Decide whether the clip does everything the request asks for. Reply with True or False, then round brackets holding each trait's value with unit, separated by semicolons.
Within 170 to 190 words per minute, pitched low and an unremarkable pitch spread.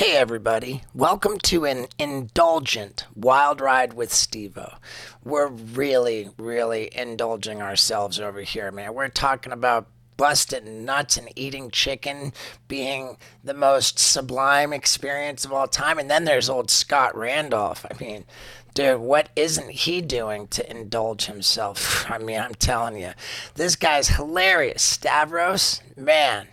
False (135 wpm; 130 Hz; 3.7 semitones)